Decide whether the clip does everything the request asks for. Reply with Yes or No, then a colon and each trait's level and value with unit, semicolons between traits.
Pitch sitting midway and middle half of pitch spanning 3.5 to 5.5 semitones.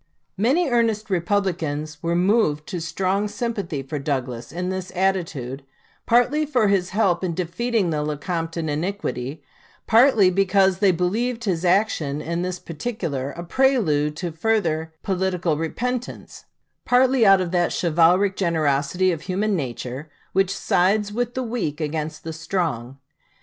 Yes: medium, 180 Hz; average, 4.8 semitones